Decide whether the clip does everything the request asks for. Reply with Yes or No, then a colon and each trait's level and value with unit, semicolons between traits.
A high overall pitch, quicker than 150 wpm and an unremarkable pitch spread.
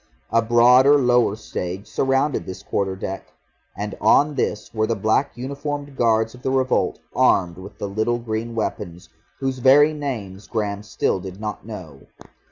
No: low, 115 Hz; average, 160 wpm; average, 4.6 semitones